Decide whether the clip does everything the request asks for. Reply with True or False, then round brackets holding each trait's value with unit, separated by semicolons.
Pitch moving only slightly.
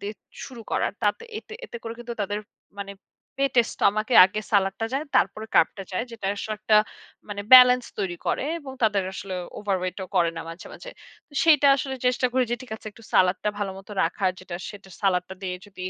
False (4.1 semitones)